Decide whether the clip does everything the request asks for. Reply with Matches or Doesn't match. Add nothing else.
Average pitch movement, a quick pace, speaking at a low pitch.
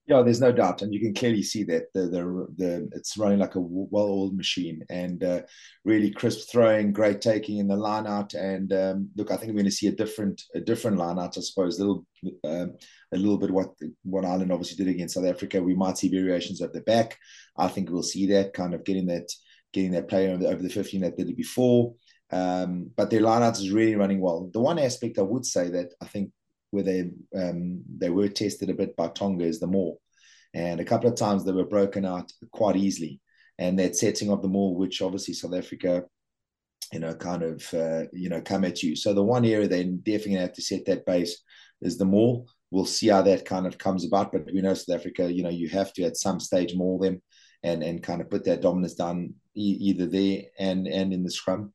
Doesn't match